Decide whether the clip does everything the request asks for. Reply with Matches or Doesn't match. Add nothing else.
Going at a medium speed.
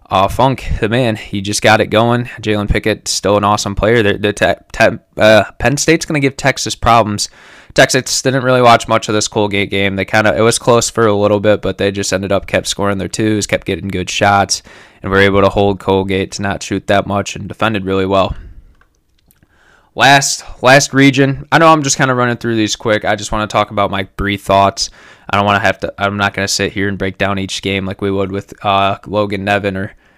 Doesn't match